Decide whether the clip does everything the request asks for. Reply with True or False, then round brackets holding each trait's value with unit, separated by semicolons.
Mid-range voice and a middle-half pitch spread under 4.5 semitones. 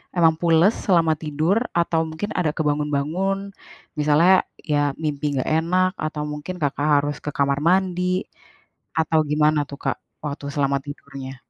True (155 Hz; 2.8 semitones)